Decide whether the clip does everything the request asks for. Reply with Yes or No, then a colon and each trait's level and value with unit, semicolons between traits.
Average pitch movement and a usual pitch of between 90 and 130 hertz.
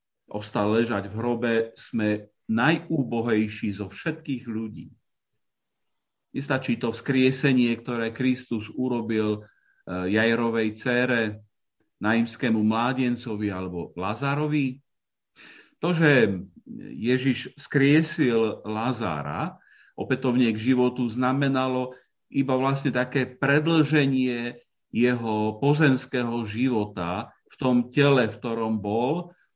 Yes: average, 3.2 semitones; low, 120 Hz